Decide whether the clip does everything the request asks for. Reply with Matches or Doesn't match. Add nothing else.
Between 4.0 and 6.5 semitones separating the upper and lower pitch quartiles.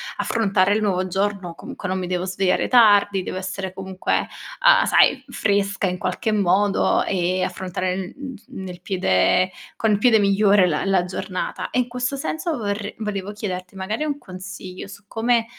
Doesn't match